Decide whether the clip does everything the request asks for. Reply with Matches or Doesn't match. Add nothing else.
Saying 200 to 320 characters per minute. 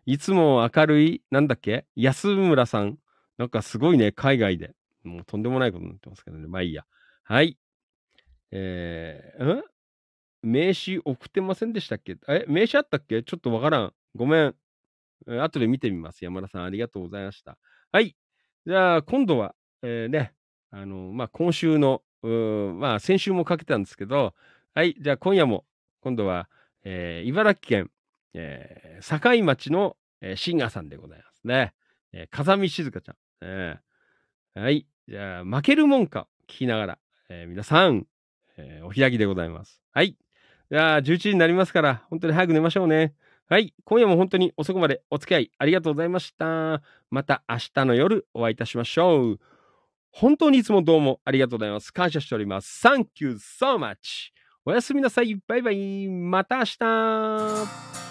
Doesn't match